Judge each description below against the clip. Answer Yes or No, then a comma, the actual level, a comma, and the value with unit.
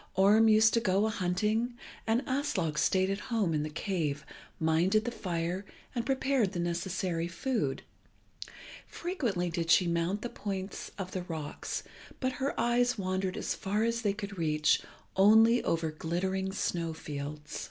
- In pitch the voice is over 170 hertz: Yes, high, 190 Hz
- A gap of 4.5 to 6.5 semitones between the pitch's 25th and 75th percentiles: Yes, average, 4.8 semitones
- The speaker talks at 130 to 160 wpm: Yes, average, 155 wpm